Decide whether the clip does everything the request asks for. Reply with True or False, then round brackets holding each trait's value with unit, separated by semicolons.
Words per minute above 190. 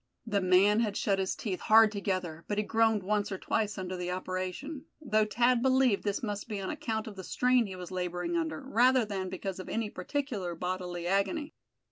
True (200 wpm)